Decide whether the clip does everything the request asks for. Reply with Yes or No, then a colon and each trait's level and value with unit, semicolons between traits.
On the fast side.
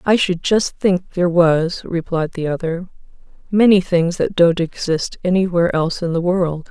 No: average, 170 wpm